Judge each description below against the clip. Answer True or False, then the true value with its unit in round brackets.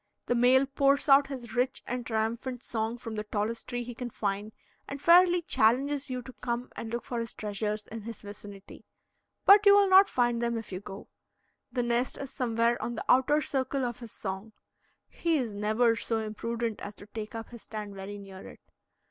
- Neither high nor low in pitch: False (235 Hz)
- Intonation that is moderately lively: True (3.1 semitones)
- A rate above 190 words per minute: True (200 wpm)